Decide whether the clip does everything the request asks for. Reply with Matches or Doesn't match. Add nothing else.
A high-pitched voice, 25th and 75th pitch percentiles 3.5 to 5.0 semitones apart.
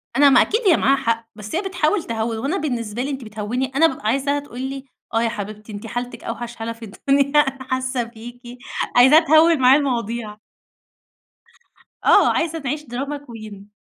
Matches